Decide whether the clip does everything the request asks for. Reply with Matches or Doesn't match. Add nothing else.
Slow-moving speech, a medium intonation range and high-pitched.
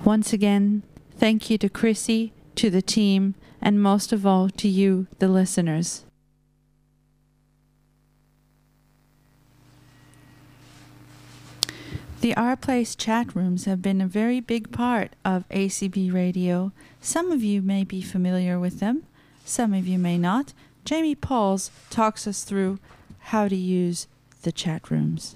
Matches